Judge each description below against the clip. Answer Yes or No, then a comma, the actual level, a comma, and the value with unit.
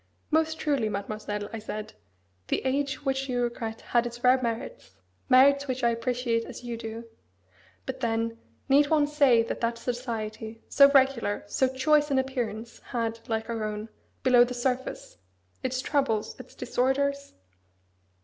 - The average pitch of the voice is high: Yes, high, 245 Hz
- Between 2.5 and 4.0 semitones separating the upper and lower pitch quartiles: Yes, average, 2.9 semitones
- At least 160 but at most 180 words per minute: No, average, 150 wpm